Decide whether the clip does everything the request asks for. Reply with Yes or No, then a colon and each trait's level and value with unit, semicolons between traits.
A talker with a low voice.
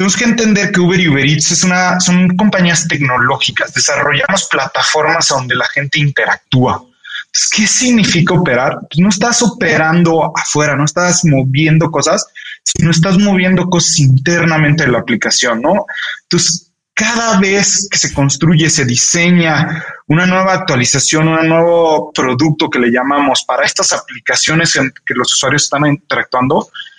No: medium, 165 Hz